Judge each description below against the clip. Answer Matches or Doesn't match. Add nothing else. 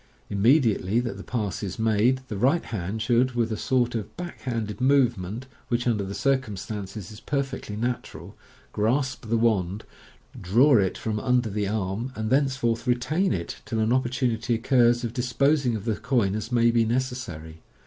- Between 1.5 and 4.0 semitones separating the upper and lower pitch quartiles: Matches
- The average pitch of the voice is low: Matches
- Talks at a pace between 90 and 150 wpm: Doesn't match